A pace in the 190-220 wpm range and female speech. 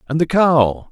No: average, 200 wpm; male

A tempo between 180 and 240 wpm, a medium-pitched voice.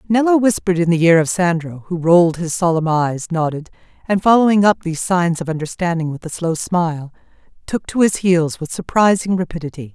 Yes: average, 185 wpm; medium, 175 Hz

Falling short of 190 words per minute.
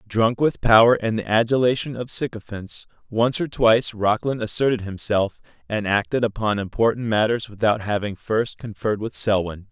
Yes: average, 155 wpm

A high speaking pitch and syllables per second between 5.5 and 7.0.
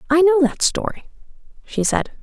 No: very high, 305 Hz; 4.8 syllables/s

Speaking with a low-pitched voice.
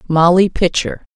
No: medium, 175 Hz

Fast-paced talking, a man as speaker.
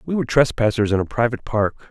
Yes: fast, 220 wpm; male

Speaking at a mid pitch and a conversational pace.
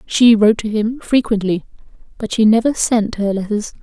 No: high, 215 Hz; average, 155 wpm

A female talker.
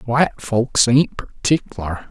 No: male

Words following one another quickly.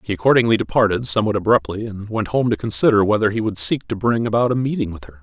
Yes: fast, 240 wpm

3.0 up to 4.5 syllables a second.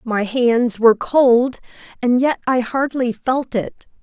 Yes: 3.7 syllables/s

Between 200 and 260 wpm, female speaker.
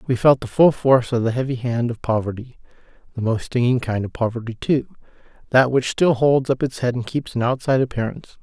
No: fast, 205 wpm; male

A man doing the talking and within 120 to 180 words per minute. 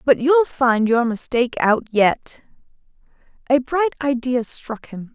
No: female; average, 140 wpm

